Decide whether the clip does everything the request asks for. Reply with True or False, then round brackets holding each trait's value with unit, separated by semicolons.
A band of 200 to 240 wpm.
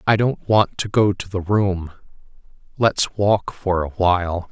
False (175 wpm)